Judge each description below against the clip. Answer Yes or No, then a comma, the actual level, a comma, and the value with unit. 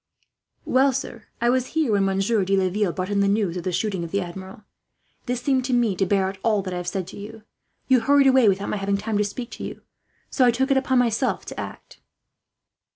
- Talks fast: Yes, fast, 240 wpm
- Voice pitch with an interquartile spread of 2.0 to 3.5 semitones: No, average, 4.4 semitones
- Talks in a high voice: Yes, high, 210 Hz